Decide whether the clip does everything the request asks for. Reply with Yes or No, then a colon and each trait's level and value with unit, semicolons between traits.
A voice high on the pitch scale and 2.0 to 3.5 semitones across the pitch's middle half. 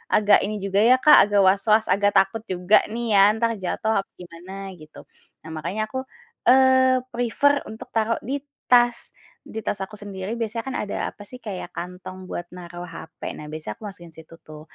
No: high, 205 Hz; average, 4.3 semitones